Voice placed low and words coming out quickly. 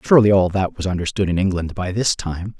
Yes: very low, 95 Hz; fast, 230 wpm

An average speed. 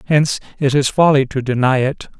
Yes: average, 190 wpm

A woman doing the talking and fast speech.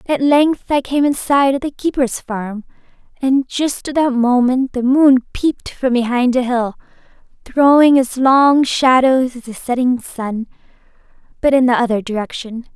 No: female; average, 165 wpm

